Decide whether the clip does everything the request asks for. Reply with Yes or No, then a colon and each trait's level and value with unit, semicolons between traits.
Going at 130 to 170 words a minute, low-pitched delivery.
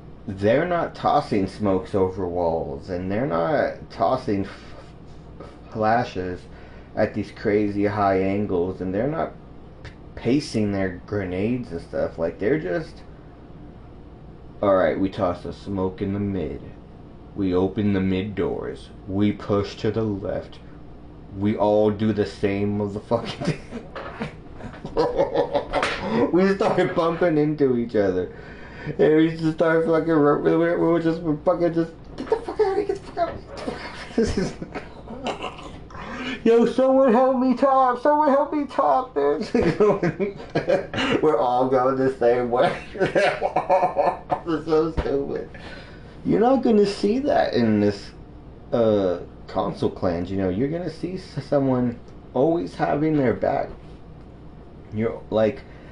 Yes: average, 140 wpm; low, 130 Hz